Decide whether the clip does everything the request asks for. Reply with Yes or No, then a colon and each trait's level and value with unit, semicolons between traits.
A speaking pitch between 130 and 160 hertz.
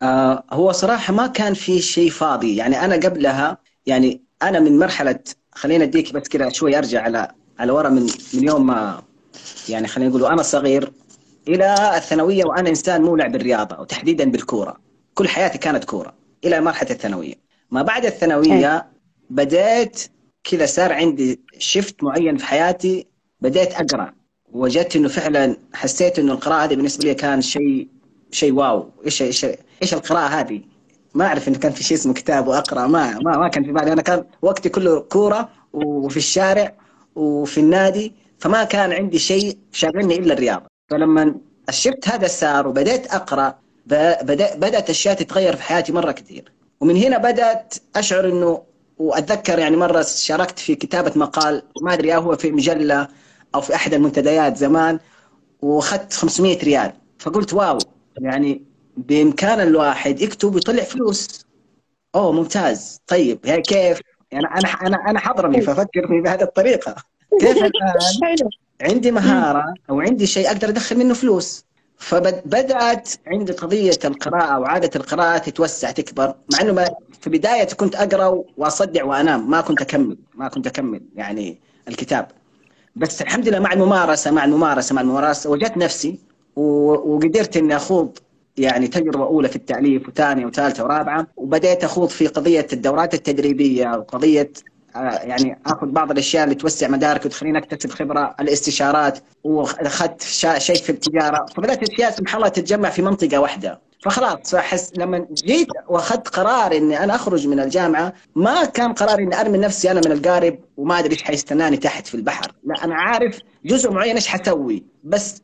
No: medium, 175 Hz